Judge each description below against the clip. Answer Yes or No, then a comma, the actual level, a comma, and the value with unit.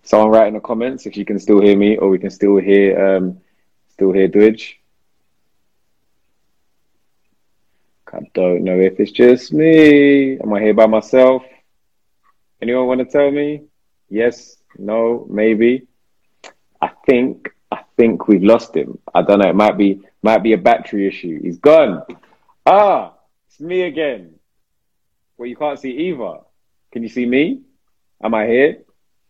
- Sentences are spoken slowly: No, average, 155 wpm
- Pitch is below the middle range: Yes, low, 110 Hz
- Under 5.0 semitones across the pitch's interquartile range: Yes, average, 4.3 semitones